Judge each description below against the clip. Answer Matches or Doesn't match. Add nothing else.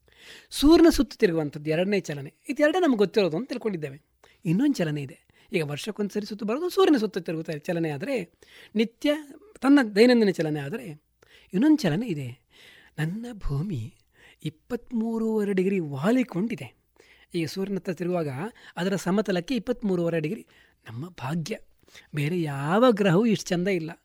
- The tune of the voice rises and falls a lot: Matches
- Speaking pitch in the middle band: Doesn't match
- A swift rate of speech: Matches